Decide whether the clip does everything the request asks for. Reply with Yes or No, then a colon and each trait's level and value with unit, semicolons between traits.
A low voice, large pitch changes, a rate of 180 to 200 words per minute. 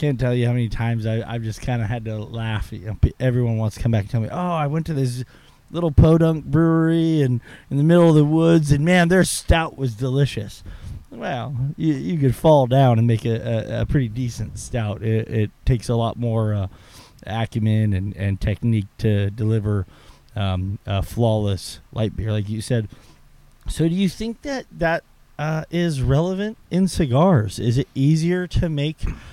Yes: low, 120 Hz; wide, 6.0 semitones; average, 190 wpm